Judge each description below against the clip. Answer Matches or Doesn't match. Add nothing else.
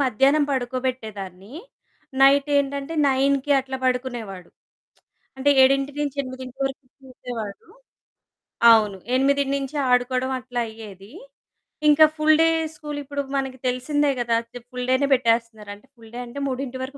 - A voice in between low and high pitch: Doesn't match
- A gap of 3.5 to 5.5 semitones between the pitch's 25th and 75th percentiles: Doesn't match